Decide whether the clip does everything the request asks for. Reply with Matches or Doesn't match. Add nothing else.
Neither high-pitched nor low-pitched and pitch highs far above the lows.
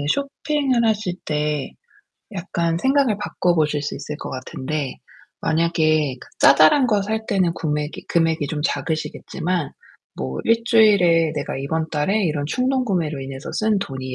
Matches